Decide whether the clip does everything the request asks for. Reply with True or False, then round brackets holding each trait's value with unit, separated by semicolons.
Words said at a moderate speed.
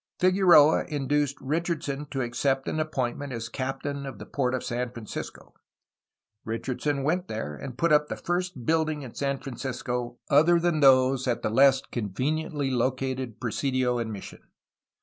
True (150 wpm)